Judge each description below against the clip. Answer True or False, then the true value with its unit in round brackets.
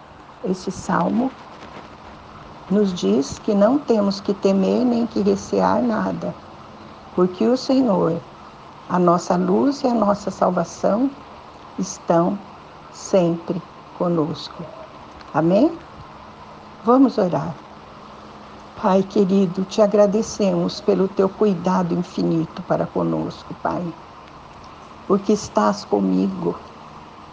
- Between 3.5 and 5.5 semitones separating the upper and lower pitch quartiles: True (4.7 semitones)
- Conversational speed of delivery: False (95 wpm)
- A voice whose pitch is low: False (190 Hz)